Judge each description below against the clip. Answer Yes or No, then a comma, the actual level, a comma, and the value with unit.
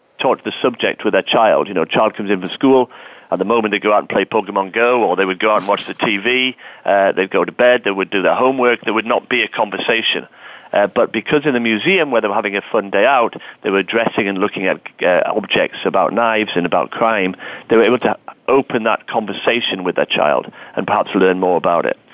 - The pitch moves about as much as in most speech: Yes, average, 3.8 semitones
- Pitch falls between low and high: No, low, 110 Hz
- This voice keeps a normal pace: No, fast, 250 wpm